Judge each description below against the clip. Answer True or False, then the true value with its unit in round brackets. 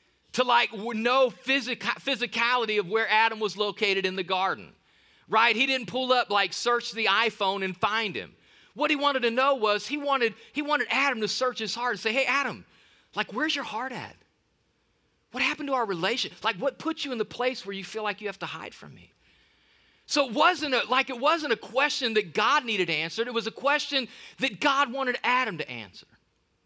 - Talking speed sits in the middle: False (210 wpm)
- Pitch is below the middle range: False (235 Hz)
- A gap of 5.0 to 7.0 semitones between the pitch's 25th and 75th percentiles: False (4.3 semitones)